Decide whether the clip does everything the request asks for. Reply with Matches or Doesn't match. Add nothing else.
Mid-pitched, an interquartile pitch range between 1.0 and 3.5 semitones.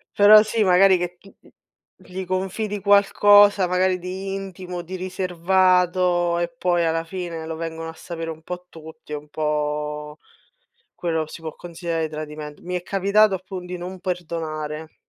Matches